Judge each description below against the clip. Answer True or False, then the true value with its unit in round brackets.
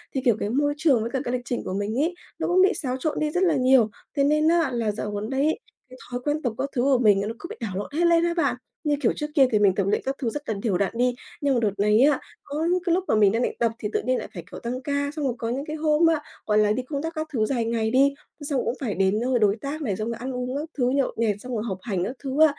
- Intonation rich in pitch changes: False (5.0 semitones)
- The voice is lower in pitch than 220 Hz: False (255 Hz)